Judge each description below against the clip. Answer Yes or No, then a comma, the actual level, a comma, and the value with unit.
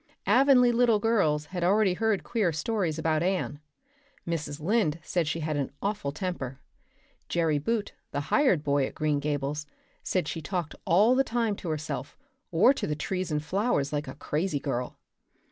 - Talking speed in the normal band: Yes, average, 170 wpm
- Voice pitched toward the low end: No, medium, 165 Hz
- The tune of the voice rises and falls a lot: Yes, wide, 5.8 semitones